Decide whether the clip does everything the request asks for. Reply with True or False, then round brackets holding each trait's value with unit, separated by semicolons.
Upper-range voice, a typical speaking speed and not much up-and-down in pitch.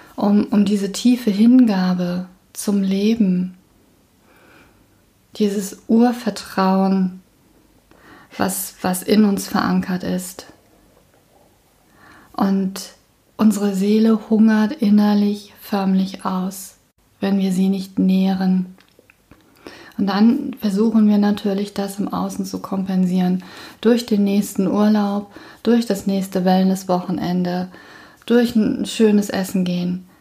False (200 Hz; 100 wpm; 2.2 semitones)